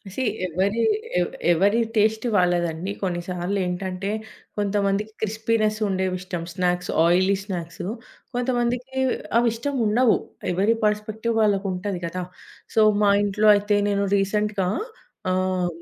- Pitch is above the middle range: Yes, high, 200 Hz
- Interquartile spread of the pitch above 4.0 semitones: No, average, 2.8 semitones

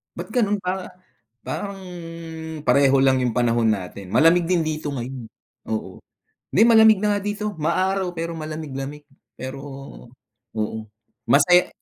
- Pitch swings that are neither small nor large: No, wide, 6.4 semitones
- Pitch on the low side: No, medium, 155 Hz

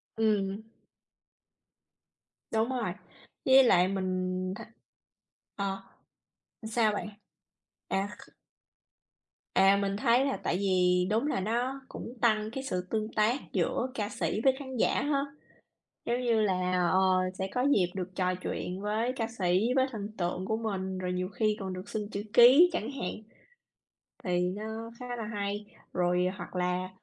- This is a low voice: No, high, 205 Hz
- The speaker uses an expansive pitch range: No, average, 3.8 semitones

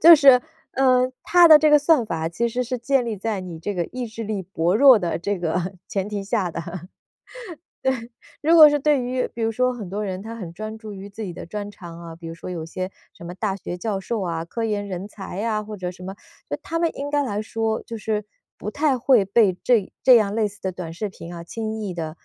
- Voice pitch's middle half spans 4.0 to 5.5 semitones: Yes, average, 4.7 semitones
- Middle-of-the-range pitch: No, high, 210 Hz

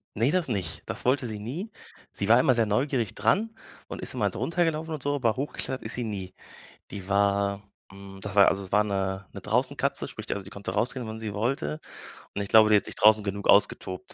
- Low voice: Yes, low, 105 Hz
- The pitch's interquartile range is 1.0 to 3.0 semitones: No, average, 4.3 semitones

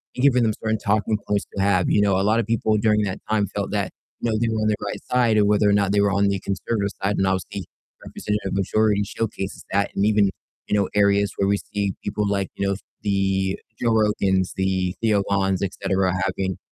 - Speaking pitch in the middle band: No, low, 100 Hz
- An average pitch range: No, narrow, 1.6 semitones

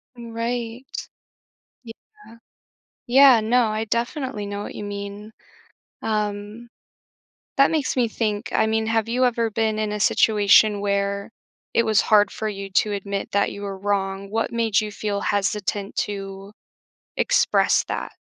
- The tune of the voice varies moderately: No, narrow, 2.3 semitones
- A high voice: Yes, high, 215 Hz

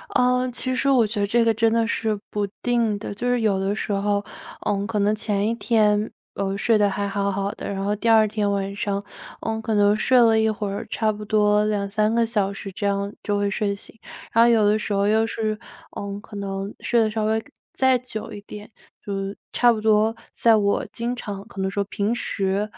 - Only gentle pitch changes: Yes, narrow, 1.8 semitones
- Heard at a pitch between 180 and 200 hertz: No, high, 210 Hz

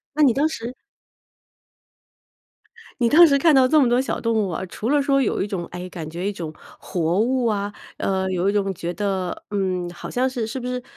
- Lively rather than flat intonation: Yes, wide, 5.7 semitones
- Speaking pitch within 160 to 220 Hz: Yes, high, 210 Hz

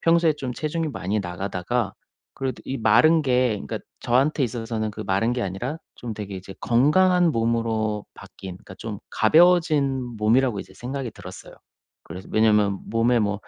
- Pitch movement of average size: Yes, average, 4.7 semitones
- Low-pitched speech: Yes, low, 115 Hz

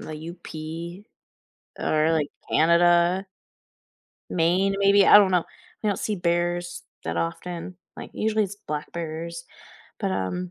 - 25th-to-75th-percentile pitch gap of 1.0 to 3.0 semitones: Yes, average, 2.7 semitones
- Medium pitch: Yes, medium, 170 Hz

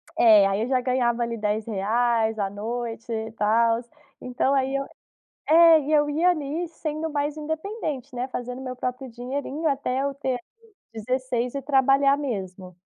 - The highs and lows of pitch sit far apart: No, average, 3.8 semitones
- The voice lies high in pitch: Yes, very high, 255 Hz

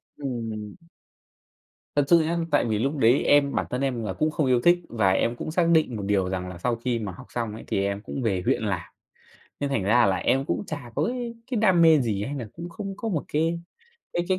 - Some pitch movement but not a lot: No, wide, 6.8 semitones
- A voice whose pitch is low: Yes, low, 125 Hz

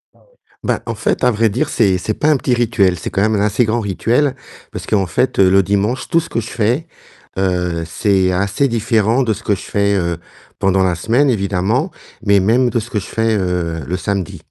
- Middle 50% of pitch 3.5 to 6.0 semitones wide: Yes, average, 3.9 semitones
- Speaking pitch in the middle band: No, low, 105 Hz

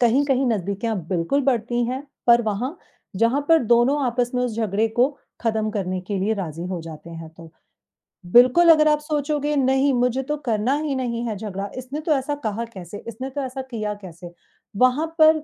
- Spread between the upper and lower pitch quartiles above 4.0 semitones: Yes, average, 4.7 semitones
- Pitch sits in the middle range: No, high, 240 Hz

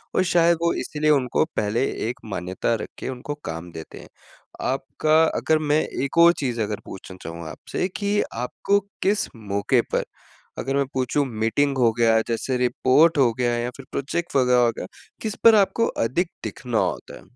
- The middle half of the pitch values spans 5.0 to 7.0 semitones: Yes, wide, 5.5 semitones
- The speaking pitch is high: No, low, 130 Hz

